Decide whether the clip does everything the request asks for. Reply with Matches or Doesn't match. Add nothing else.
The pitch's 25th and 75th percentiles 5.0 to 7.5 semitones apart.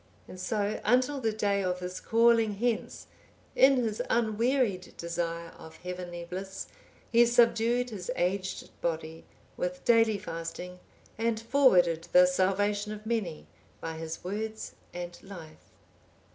Doesn't match